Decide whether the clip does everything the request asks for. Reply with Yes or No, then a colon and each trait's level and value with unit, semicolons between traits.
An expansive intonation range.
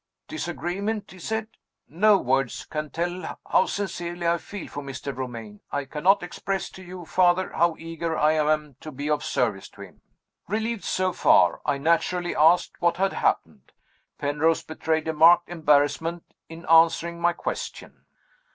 No: average, 2.9 semitones